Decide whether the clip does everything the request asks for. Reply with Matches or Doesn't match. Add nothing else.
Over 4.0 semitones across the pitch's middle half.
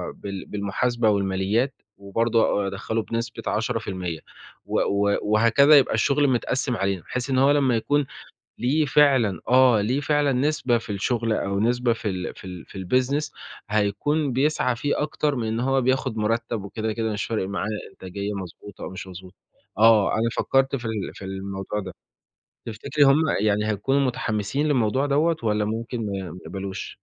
Matches